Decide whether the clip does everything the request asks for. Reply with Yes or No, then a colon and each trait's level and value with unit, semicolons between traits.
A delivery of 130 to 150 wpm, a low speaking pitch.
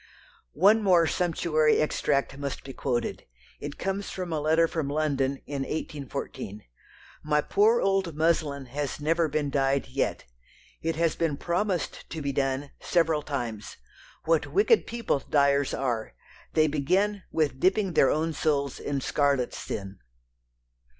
No: average, 140 wpm; medium, 150 Hz